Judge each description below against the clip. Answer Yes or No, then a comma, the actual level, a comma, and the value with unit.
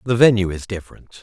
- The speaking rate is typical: Yes, average, 195 wpm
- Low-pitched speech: Yes, low, 105 Hz